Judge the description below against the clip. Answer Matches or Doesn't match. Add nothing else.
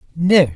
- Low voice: Doesn't match